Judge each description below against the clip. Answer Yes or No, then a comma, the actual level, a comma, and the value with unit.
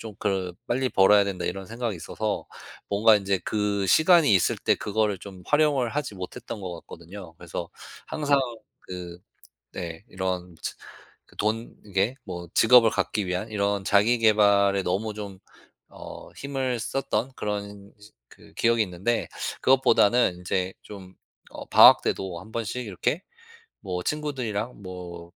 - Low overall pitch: Yes, low, 100 Hz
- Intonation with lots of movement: No, average, 3.7 semitones